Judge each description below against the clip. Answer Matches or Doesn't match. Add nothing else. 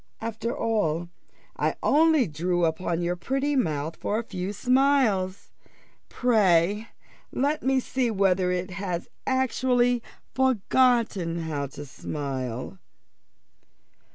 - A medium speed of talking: Doesn't match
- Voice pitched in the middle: Doesn't match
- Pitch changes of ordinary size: Doesn't match